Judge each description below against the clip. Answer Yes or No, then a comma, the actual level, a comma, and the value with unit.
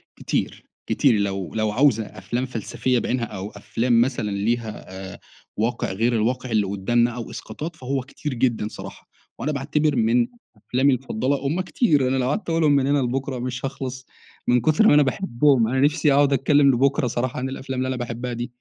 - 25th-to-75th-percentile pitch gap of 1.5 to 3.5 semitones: Yes, average, 3.1 semitones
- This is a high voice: No, low, 125 Hz